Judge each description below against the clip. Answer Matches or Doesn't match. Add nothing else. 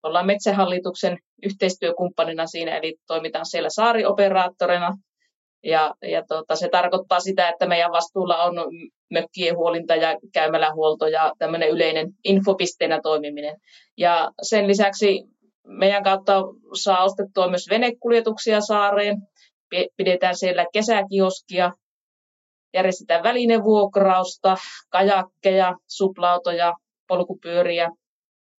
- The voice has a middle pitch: Matches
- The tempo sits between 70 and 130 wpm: Matches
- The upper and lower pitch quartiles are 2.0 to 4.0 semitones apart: Matches